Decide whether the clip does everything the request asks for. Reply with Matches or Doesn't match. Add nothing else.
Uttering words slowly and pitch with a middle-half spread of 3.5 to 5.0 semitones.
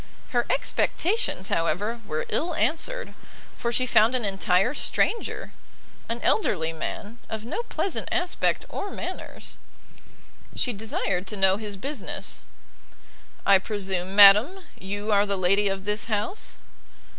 Matches